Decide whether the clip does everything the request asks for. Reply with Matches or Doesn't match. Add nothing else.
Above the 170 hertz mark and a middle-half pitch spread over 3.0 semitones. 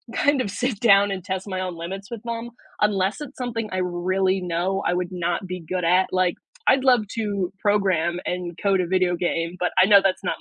Doesn't match